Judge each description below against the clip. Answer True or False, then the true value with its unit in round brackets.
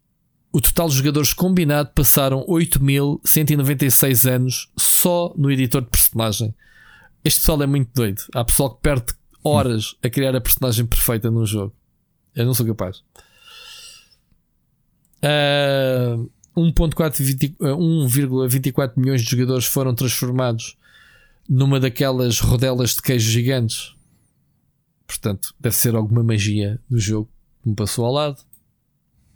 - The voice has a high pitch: False (130 Hz)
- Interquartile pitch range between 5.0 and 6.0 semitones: False (3.6 semitones)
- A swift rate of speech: False (120 wpm)